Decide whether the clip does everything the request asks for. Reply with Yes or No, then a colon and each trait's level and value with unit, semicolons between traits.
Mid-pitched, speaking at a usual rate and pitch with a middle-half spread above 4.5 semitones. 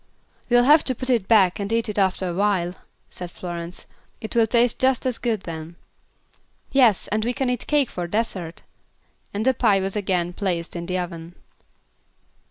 No: high, 205 Hz; average, 180 wpm; average, 5.0 semitones